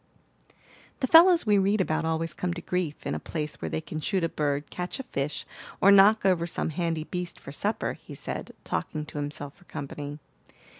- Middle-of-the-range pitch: Yes, medium, 165 Hz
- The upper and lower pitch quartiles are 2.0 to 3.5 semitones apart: No, average, 4.3 semitones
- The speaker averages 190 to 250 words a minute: Yes, average, 200 wpm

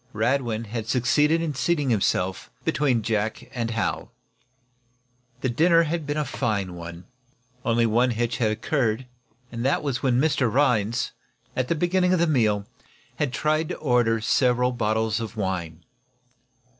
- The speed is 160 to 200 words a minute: No, average, 145 wpm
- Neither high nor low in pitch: No, low, 120 Hz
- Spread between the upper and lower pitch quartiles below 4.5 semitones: No, average, 4.8 semitones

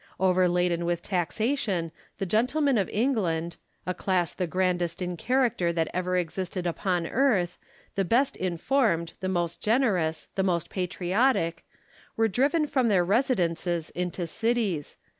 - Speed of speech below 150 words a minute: Yes, average, 140 wpm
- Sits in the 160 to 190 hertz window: Yes, medium, 185 Hz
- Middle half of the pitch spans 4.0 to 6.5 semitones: Yes, average, 4.6 semitones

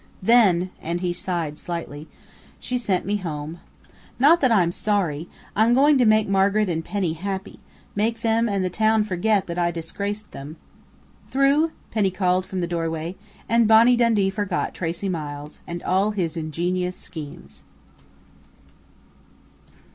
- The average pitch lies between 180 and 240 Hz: Yes, medium, 185 Hz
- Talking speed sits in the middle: Yes, average, 155 wpm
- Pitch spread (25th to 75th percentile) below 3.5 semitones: No, average, 4.2 semitones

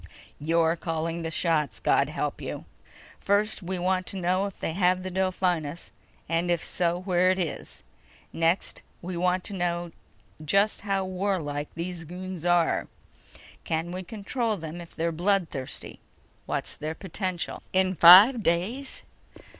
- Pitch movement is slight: Yes, narrow, 2.1 semitones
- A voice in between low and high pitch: Yes, medium, 180 Hz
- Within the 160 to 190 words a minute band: No, average, 145 wpm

